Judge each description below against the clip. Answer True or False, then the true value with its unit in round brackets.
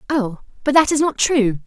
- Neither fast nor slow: False (215 wpm)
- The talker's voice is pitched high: True (260 Hz)